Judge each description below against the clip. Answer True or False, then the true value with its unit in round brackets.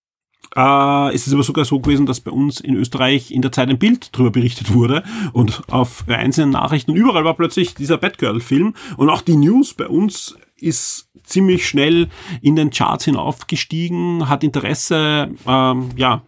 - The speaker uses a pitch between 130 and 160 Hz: True (140 Hz)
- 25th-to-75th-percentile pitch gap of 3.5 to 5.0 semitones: True (4.2 semitones)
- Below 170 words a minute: False (175 wpm)